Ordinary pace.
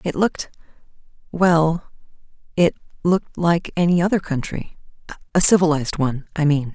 No: slow, 105 wpm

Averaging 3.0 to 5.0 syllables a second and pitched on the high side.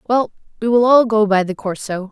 Yes: 4.9 syllables/s; high, 215 Hz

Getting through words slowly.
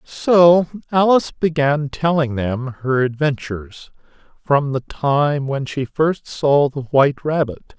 Yes: slow, 130 wpm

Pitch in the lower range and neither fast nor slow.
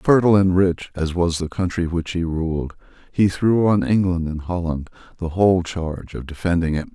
Yes: very low, 85 Hz; average, 190 wpm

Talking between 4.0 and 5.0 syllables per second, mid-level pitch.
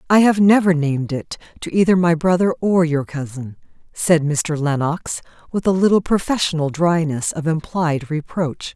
Yes: 4.7 syllables/s; medium, 165 Hz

